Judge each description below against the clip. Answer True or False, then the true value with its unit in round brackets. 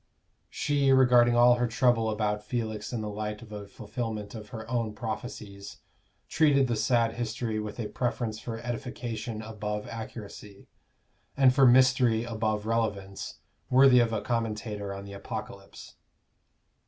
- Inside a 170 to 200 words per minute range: False (140 wpm)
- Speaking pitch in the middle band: False (115 Hz)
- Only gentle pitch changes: True (2.3 semitones)